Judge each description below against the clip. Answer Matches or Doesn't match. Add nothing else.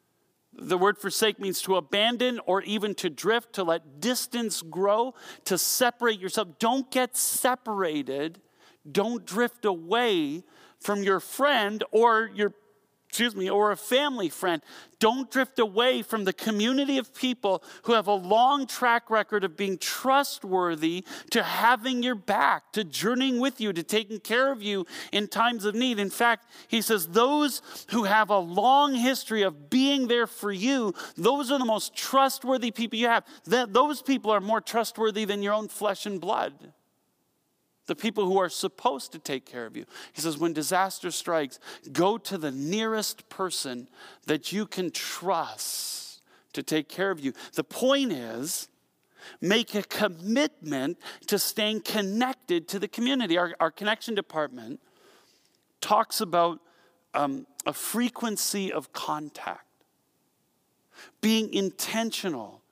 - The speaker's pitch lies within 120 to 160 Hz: Doesn't match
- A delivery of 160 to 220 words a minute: Doesn't match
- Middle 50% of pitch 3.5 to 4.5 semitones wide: Matches